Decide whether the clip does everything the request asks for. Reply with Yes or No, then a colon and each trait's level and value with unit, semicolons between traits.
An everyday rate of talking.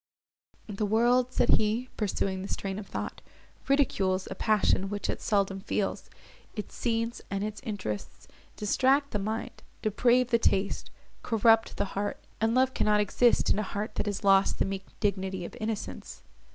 Yes: average, 165 wpm